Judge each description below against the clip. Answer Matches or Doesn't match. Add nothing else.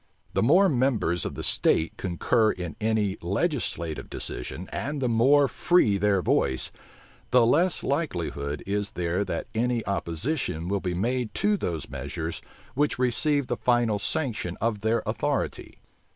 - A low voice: Matches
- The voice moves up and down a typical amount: Doesn't match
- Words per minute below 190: Matches